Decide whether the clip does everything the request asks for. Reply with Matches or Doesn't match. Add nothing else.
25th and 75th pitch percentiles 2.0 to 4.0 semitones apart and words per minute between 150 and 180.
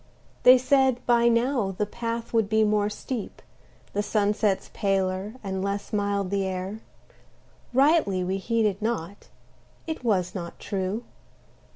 Doesn't match